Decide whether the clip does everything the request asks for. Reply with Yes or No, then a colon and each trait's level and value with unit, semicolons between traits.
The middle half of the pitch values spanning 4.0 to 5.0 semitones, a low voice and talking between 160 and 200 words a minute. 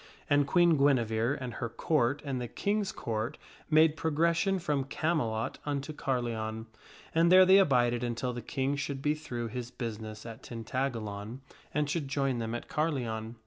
Yes: average, 4.5 semitones; low, 130 Hz; average, 165 wpm